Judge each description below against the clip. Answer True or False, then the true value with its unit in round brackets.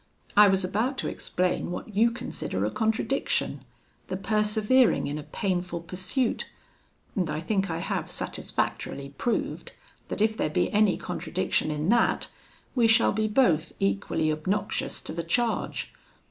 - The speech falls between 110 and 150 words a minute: True (145 wpm)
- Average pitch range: True (4.5 semitones)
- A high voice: True (200 Hz)